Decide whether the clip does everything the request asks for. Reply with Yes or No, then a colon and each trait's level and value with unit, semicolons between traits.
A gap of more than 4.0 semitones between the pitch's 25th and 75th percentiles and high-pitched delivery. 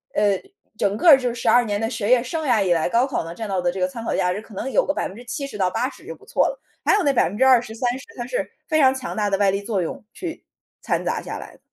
Yes: average, 4.7 semitones; high, 230 Hz